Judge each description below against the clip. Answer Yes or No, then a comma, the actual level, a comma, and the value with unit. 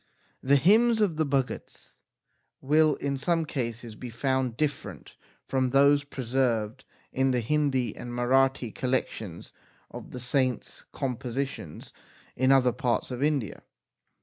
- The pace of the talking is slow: Yes, slow, 130 wpm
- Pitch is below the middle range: Yes, low, 130 Hz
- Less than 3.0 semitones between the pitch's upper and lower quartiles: Yes, narrow, 2.5 semitones